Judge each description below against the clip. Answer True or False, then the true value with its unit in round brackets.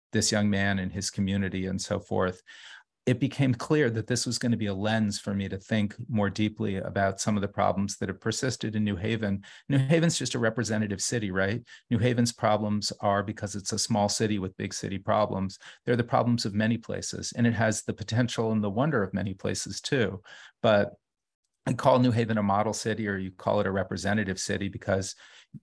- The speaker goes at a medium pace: False (215 wpm)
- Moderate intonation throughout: True (3.0 semitones)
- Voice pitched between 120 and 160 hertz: False (105 Hz)